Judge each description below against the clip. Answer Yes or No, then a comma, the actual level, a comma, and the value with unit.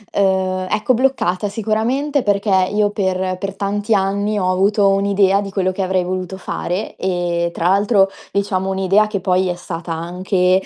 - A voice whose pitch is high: Yes, high, 195 Hz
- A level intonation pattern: Yes, narrow, 1.8 semitones